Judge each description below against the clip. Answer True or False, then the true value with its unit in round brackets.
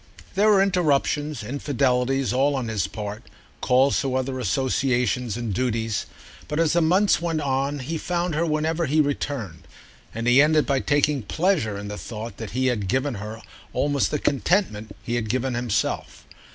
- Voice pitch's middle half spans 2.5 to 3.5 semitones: False (4.6 semitones)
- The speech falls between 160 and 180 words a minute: True (170 wpm)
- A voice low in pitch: True (130 Hz)